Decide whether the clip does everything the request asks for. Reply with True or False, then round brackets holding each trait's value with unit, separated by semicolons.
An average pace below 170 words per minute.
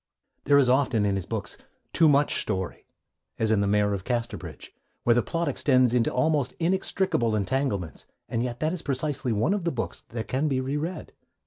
False (195 wpm)